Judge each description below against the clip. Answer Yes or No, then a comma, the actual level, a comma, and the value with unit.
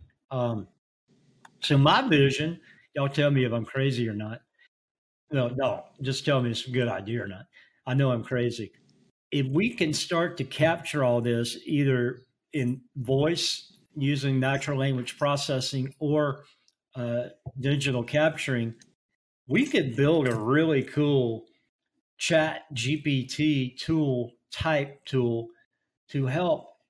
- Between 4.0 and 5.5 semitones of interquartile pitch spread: No, average, 3.1 semitones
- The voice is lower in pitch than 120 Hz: No, low, 135 Hz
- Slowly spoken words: Yes, slow, 130 wpm